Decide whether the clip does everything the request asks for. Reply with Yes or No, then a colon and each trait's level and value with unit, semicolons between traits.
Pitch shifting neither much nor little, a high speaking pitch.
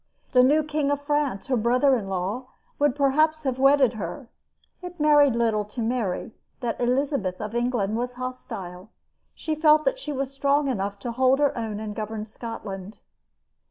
Yes: average, 4.8 semitones; very high, 250 Hz